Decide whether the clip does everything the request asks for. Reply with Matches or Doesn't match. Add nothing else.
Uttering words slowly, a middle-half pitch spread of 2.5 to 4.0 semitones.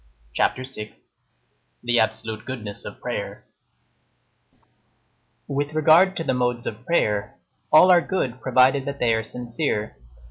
Doesn't match